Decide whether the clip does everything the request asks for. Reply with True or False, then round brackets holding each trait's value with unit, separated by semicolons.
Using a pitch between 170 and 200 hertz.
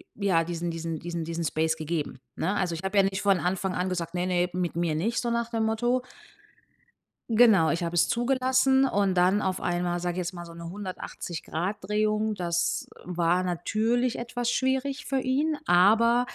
True (185 Hz)